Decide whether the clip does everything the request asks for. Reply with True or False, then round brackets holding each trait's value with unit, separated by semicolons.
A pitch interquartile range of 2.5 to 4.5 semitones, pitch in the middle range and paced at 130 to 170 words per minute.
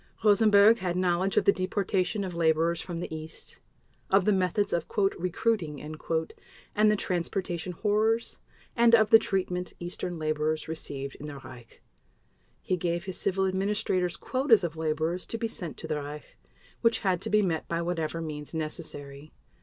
True (4.0 semitones; 180 Hz; 160 wpm)